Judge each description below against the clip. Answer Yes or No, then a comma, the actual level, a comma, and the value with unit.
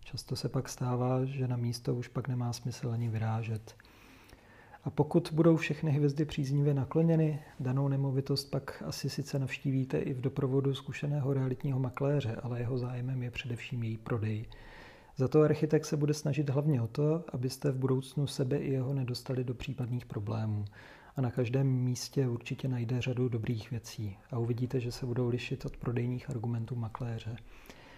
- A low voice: Yes, low, 130 Hz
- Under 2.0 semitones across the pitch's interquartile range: No, average, 2.7 semitones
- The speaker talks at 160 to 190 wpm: Yes, average, 165 wpm